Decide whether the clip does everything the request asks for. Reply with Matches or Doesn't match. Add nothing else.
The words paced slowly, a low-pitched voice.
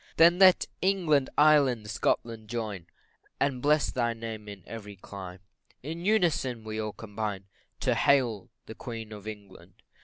Doesn't match